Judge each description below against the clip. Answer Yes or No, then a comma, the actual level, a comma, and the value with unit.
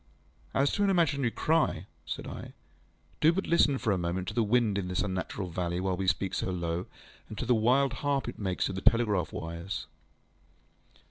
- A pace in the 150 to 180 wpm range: No, average, 195 wpm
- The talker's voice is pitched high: No, low, 100 Hz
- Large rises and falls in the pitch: Yes, wide, 6.5 semitones